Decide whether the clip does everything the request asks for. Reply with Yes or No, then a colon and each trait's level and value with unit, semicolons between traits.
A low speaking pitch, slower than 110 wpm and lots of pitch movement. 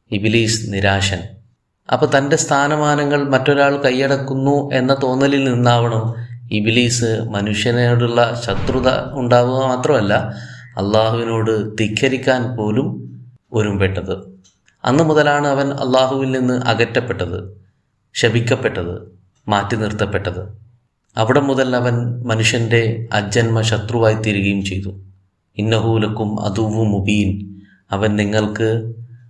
No: low, 115 Hz; average, 80 wpm; average, 3.5 semitones